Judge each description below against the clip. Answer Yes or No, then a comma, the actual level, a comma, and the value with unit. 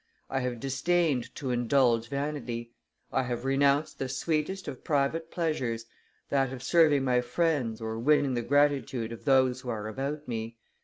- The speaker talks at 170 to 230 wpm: No, average, 160 wpm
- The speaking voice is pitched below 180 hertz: Yes, low, 135 Hz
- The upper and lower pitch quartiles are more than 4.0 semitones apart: No, average, 3.4 semitones